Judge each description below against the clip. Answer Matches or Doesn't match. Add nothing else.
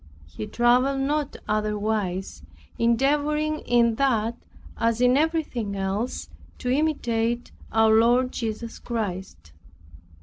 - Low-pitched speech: Doesn't match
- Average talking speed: Doesn't match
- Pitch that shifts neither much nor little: Matches